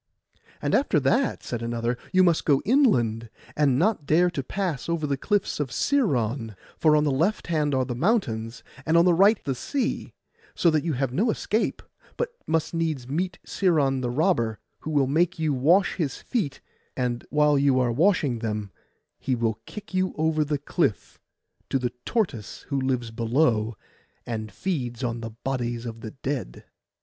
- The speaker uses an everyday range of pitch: No, wide, 5.9 semitones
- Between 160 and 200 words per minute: Yes, average, 180 wpm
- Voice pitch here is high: No, medium, 140 Hz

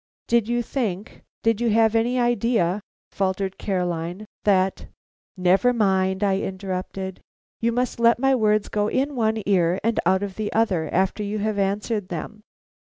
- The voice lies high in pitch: Yes, high, 205 Hz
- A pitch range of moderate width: Yes, average, 3.2 semitones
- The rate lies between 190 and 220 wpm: No, average, 170 wpm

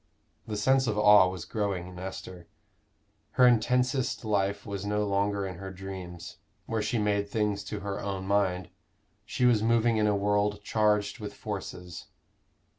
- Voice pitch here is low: Yes, low, 100 Hz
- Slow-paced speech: No, average, 160 wpm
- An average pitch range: No, narrow, 1.9 semitones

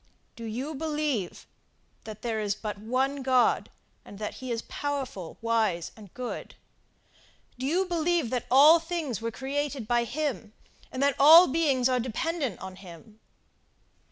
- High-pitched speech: Yes, very high, 255 Hz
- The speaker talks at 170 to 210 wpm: No, average, 150 wpm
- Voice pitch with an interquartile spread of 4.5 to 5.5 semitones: Yes, average, 4.9 semitones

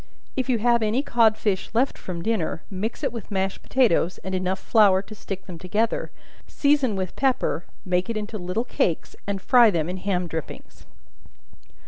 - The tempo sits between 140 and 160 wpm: No, average, 175 wpm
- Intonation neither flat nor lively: Yes, average, 3.9 semitones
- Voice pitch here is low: No, high, 205 Hz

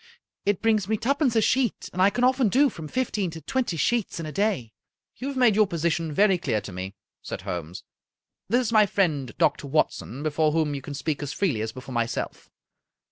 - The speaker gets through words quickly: Yes, fast, 215 wpm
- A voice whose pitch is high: No, medium, 175 Hz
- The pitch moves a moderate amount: No, wide, 7.6 semitones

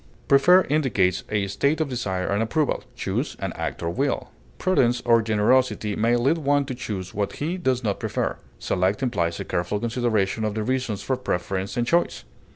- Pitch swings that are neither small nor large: Yes, average, 5.0 semitones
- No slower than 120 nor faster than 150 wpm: No, average, 180 wpm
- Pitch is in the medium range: No, low, 115 Hz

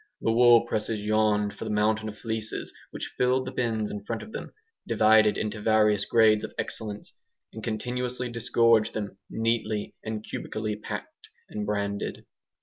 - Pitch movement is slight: Yes, narrow, 1.6 semitones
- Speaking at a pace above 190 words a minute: No, average, 155 wpm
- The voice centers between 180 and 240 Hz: No, low, 110 Hz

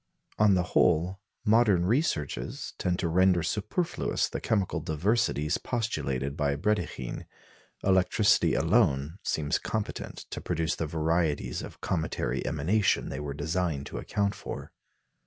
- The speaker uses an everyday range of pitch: Yes, average, 5.0 semitones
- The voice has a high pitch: No, very low, 85 Hz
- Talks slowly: Yes, slow, 125 wpm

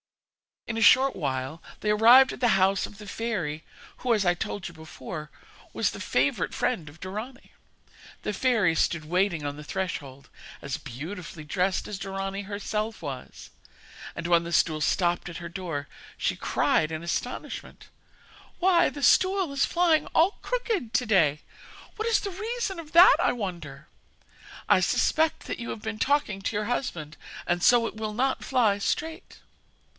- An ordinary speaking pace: Yes, average, 170 wpm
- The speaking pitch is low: No, high, 200 Hz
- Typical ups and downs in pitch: No, wide, 7.1 semitones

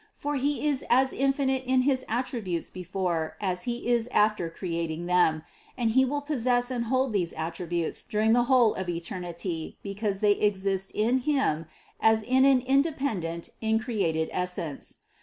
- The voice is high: Yes, high, 220 Hz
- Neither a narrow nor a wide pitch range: No, wide, 6.5 semitones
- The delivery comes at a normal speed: Yes, average, 160 wpm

